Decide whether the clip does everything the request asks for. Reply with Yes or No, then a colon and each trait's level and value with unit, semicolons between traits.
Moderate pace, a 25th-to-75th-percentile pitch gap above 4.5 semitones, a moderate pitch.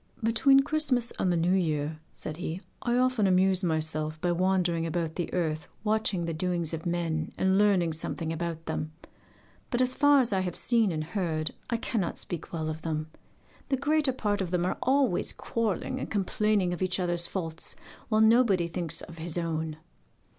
Yes: average, 180 wpm; average, 5.0 semitones; medium, 180 Hz